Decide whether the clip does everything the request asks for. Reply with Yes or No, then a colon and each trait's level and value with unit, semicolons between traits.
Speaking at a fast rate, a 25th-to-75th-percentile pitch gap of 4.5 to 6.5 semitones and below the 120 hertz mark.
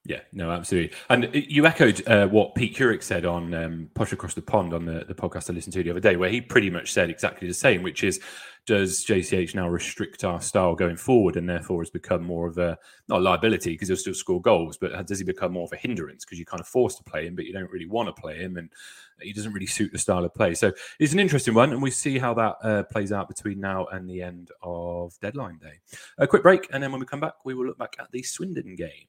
Yes: fast, 270 wpm; average, 5.2 semitones; very low, 95 Hz